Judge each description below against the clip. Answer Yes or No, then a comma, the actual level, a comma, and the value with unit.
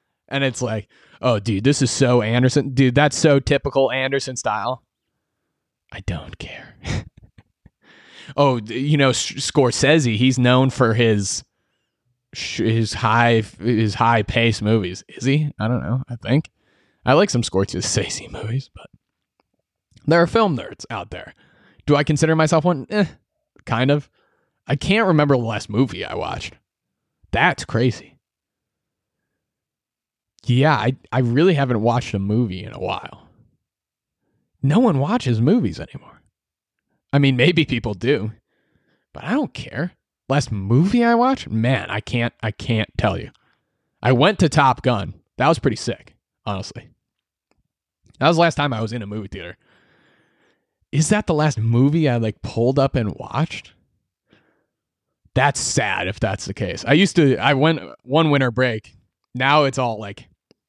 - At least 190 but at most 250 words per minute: No, average, 150 wpm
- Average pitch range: Yes, average, 4.2 semitones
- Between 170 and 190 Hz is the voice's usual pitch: No, low, 125 Hz